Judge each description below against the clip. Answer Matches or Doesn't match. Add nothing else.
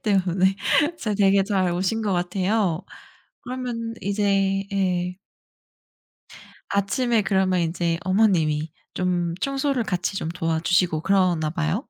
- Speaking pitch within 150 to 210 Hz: Matches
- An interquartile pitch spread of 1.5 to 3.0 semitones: Matches